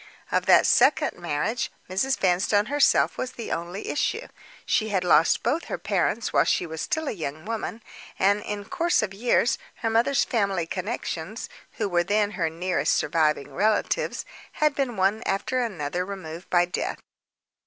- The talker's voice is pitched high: Yes, high, 200 Hz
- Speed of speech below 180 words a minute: Yes, average, 165 wpm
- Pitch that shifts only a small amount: No, average, 4.7 semitones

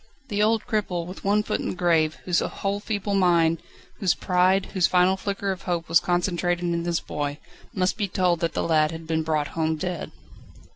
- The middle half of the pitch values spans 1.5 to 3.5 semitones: Yes, average, 2.9 semitones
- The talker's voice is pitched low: No, medium, 180 Hz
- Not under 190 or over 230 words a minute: Yes, average, 200 wpm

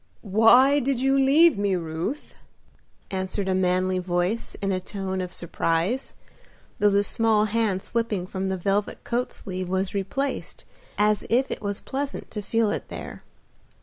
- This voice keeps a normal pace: Yes, average, 155 wpm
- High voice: Yes, high, 200 Hz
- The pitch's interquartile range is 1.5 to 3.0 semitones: No, average, 3.7 semitones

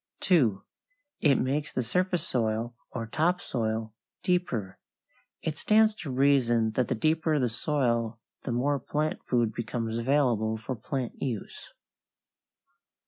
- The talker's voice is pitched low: Yes, low, 125 Hz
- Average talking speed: No, slow, 125 wpm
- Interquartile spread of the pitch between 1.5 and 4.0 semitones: No, average, 4.6 semitones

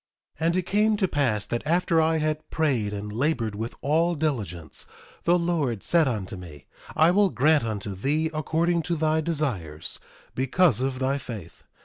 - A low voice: No, medium, 150 Hz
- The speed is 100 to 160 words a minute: No, average, 170 wpm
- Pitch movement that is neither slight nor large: No, wide, 6.8 semitones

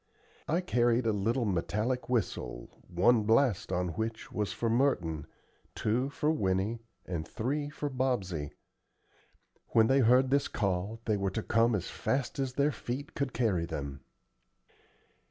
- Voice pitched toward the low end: Yes, low, 115 Hz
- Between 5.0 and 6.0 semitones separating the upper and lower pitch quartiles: Yes, wide, 5.4 semitones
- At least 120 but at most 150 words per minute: Yes, average, 145 wpm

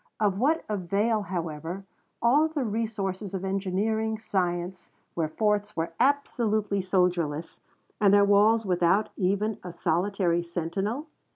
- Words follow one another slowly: Yes, slow, 120 wpm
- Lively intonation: No, average, 3.4 semitones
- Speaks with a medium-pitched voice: No, high, 200 Hz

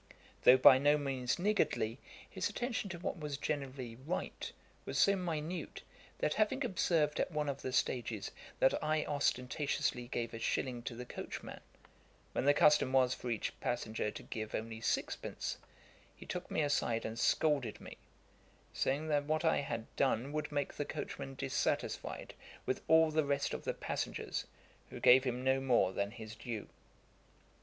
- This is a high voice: No, low, 135 Hz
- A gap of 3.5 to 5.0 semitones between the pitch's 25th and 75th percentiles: Yes, average, 4.1 semitones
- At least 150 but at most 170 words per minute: Yes, average, 165 wpm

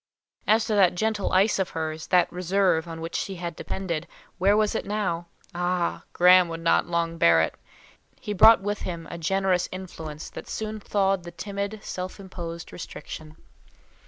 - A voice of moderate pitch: Yes, medium, 180 Hz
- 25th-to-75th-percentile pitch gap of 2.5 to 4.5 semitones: Yes, average, 2.9 semitones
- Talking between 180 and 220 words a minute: No, average, 165 wpm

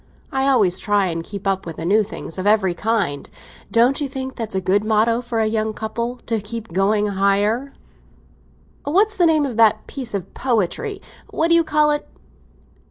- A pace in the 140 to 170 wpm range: No, average, 180 wpm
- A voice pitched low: No, high, 220 Hz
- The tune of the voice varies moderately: Yes, average, 4.8 semitones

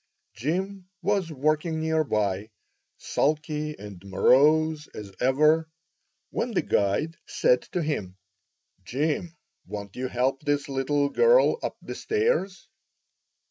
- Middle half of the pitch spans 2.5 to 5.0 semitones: Yes, average, 4.4 semitones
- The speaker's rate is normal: No, slow, 115 wpm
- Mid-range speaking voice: Yes, medium, 150 Hz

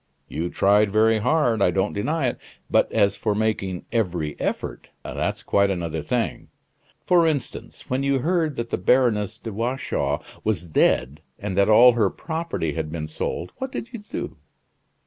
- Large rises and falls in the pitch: Yes, wide, 6.1 semitones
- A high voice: No, low, 110 Hz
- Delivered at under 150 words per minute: No, average, 165 wpm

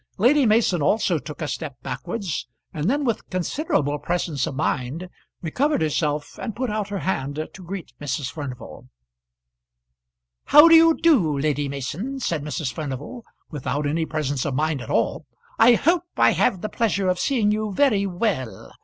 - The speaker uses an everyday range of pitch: No, wide, 7.3 semitones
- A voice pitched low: No, medium, 170 Hz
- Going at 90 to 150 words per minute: No, average, 165 wpm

